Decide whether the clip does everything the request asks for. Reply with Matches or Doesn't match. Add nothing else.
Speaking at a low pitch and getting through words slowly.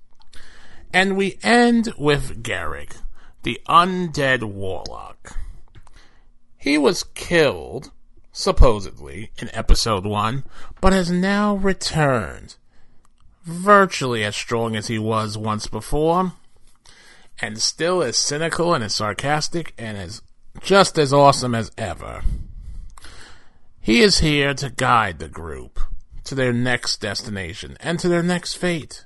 Matches